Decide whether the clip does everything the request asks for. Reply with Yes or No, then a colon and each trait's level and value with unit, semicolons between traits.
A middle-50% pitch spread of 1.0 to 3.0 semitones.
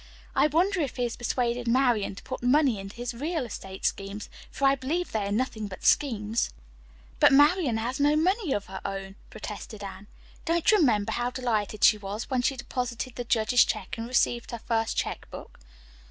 No: average, 4.4 semitones